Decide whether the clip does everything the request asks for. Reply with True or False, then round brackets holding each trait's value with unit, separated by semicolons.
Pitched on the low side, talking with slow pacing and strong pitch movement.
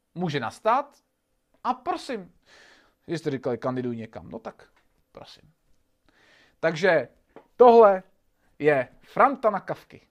False (190 Hz; 100 wpm; 9.0 semitones)